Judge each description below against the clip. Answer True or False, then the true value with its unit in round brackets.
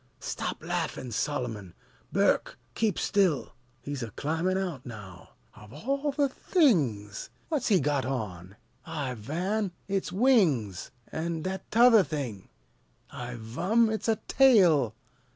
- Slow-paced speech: True (125 wpm)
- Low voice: False (155 Hz)